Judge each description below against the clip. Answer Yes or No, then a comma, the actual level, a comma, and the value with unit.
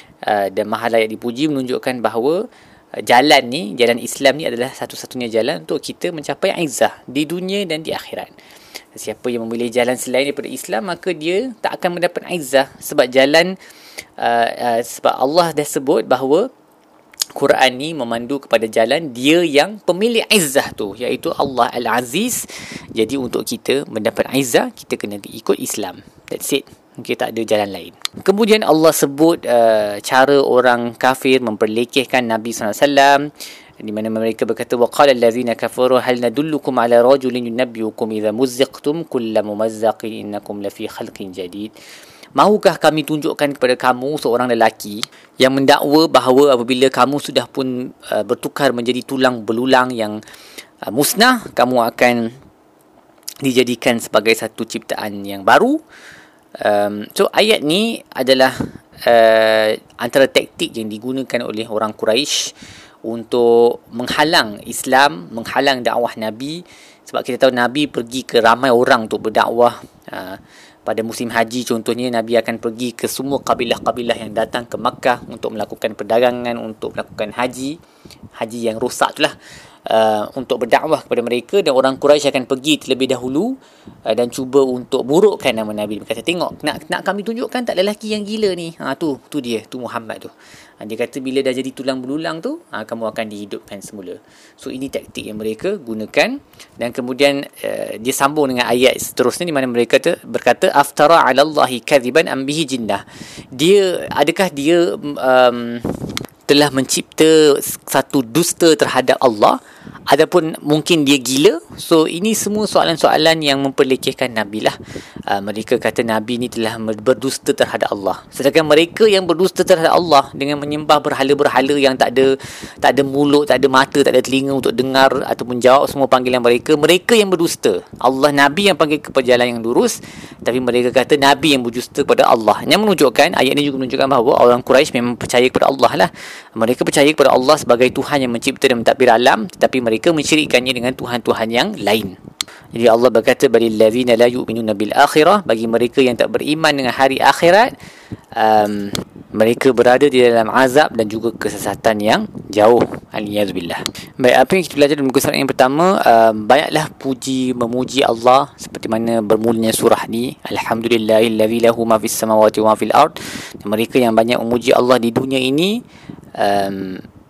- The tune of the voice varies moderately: Yes, average, 3.9 semitones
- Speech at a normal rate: No, fast, 160 wpm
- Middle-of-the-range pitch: No, low, 130 Hz